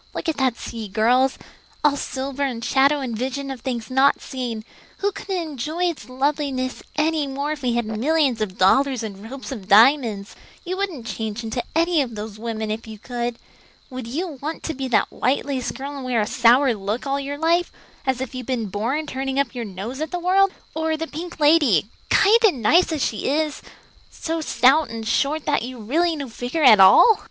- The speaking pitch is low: No, very high, 265 Hz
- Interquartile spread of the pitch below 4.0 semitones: No, average, 4.6 semitones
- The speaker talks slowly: No, fast, 205 wpm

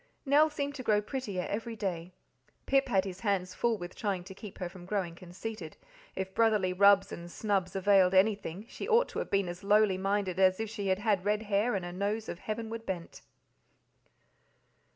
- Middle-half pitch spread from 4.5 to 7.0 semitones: No, average, 2.9 semitones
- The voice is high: Yes, high, 200 Hz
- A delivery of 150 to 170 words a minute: No, average, 195 wpm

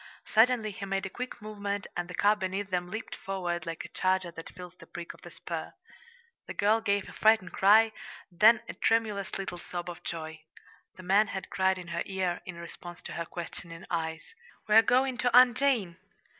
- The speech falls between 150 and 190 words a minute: No, average, 200 wpm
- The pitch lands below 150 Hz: No, high, 190 Hz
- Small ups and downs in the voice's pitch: No, average, 3.6 semitones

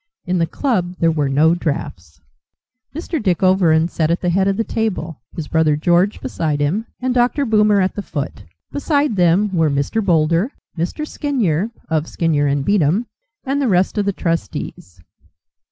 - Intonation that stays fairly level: No, average, 5.1 semitones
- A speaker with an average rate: Yes, average, 170 wpm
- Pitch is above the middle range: No, medium, 175 Hz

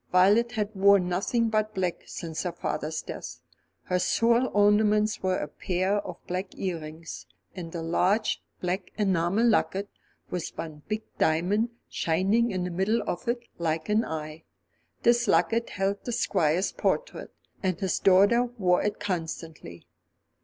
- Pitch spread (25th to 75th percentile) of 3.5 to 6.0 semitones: Yes, average, 3.8 semitones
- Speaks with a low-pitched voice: No, high, 190 Hz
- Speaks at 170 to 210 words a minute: No, average, 145 wpm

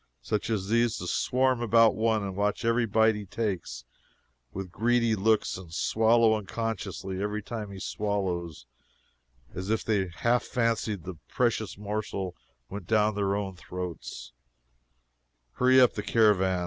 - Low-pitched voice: Yes, low, 105 Hz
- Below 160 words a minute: Yes, average, 145 wpm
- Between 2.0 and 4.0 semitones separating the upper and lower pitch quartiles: Yes, average, 3.0 semitones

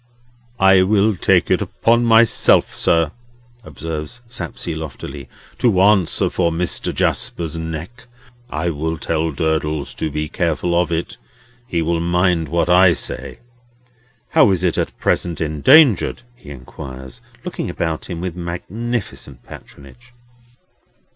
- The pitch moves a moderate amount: Yes, average, 3.4 semitones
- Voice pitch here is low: Yes, very low, 85 Hz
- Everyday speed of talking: No, slow, 130 wpm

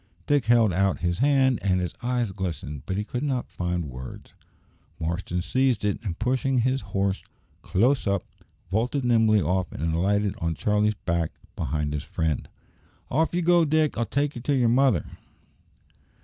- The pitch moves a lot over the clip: Yes, wide, 6.5 semitones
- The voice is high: No, low, 105 Hz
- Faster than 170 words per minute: No, average, 165 wpm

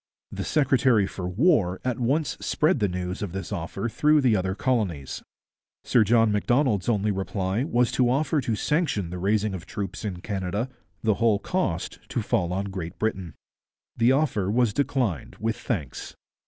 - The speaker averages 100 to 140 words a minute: No, average, 170 wpm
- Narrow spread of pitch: No, average, 4.8 semitones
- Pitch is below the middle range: Yes, low, 105 Hz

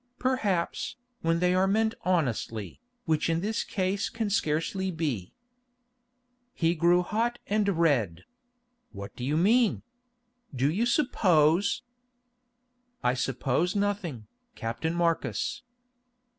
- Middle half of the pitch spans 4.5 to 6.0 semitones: Yes, average, 5.3 semitones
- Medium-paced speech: No, slow, 110 wpm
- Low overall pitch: No, medium, 170 Hz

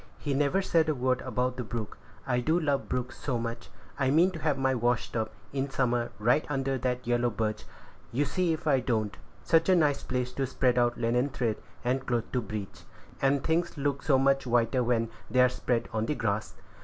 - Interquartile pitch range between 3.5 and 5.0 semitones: No, average, 2.9 semitones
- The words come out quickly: Yes, fast, 210 wpm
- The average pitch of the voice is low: Yes, low, 125 Hz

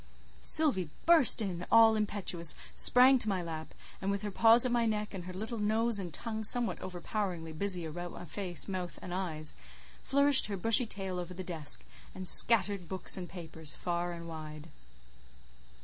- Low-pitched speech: No, high, 190 Hz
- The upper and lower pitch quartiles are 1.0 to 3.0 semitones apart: No, average, 4.2 semitones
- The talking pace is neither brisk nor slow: Yes, average, 175 wpm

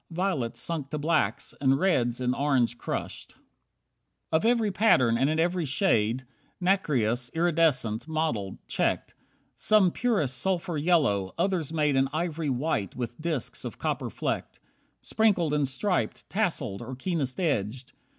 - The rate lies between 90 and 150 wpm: Yes, average, 140 wpm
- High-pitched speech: No, medium, 150 Hz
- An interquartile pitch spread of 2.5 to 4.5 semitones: No, wide, 5.6 semitones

